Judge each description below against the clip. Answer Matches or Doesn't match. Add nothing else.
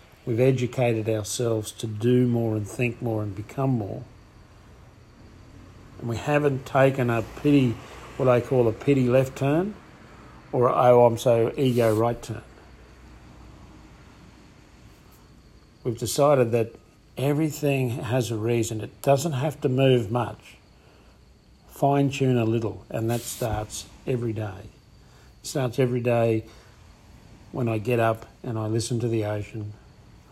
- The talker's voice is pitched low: Matches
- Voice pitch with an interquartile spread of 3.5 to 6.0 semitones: Doesn't match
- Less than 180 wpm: Matches